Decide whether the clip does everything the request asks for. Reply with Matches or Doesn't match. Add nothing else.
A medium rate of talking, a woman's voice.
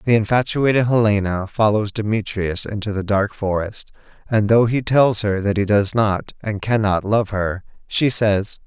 Doesn't match